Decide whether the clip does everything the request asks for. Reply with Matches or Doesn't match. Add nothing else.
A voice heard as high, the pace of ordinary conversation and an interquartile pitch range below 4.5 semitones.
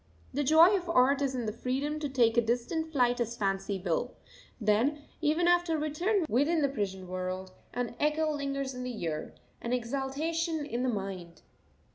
Doesn't match